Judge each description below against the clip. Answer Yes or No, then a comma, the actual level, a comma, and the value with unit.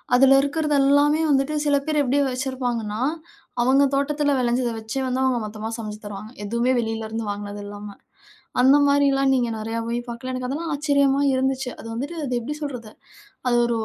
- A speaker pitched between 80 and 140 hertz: No, very high, 255 Hz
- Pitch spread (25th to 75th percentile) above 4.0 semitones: No, average, 3.6 semitones